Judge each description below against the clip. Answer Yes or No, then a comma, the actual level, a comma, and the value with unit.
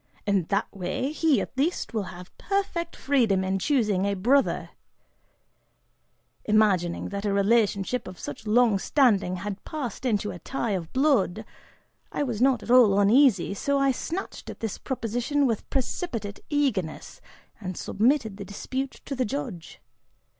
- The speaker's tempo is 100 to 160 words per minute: Yes, average, 150 wpm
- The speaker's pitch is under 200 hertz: No, high, 220 Hz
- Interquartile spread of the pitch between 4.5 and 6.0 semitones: Yes, average, 5.3 semitones